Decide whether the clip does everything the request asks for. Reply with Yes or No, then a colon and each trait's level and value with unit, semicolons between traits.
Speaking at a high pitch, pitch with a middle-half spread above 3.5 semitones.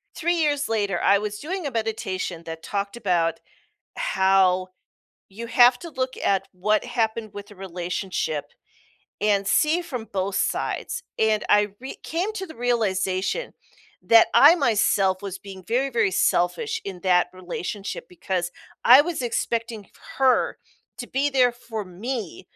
Yes: high, 215 Hz; average, 5.1 semitones